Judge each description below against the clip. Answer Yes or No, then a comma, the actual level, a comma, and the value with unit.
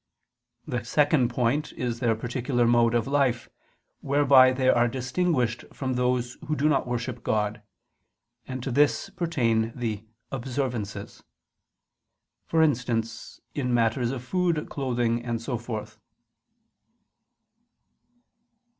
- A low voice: Yes, low, 125 Hz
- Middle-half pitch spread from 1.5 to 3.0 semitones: Yes, narrow, 2.5 semitones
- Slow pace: Yes, slow, 115 wpm